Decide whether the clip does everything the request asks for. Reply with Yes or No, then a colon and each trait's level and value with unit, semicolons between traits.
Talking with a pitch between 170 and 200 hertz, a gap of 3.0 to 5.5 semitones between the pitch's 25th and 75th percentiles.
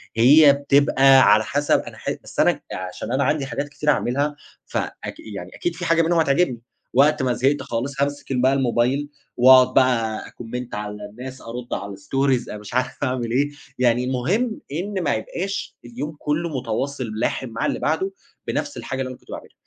No: low, 130 Hz; average, 3.4 semitones